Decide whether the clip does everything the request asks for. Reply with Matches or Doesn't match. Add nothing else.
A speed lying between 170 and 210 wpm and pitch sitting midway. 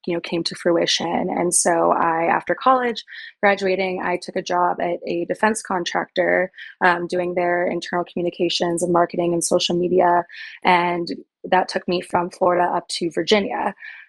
Doesn't match